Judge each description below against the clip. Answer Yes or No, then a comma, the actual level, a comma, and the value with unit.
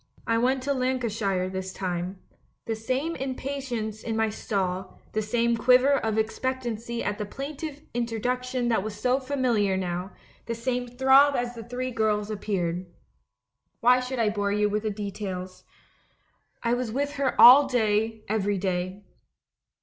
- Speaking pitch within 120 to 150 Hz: No, high, 225 Hz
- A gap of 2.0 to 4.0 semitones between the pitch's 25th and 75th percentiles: Yes, average, 3.6 semitones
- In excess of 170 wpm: No, average, 150 wpm